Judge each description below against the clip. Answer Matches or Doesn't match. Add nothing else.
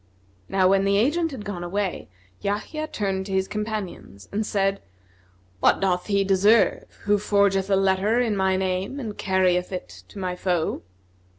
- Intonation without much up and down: Matches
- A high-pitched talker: Matches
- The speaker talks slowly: Doesn't match